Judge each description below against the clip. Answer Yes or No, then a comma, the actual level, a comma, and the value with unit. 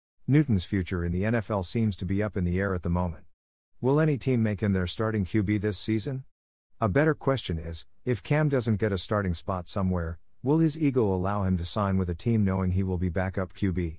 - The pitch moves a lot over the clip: No, average, 3.8 semitones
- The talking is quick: Yes, fast, 225 wpm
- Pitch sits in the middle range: No, low, 100 Hz